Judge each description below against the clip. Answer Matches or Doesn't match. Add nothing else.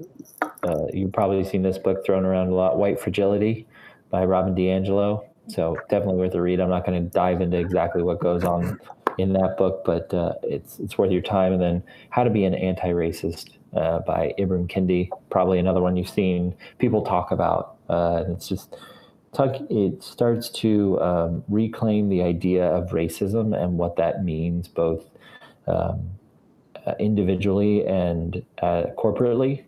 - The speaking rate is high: Doesn't match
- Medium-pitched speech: Doesn't match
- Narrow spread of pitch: Matches